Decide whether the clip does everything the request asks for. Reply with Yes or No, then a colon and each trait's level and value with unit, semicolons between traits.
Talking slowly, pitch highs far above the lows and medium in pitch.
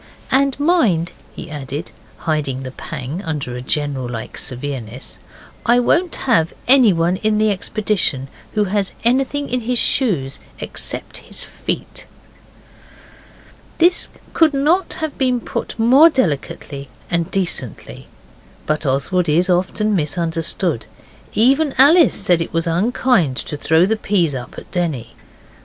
Yes: slow, 130 wpm; wide, 8.7 semitones; medium, 180 Hz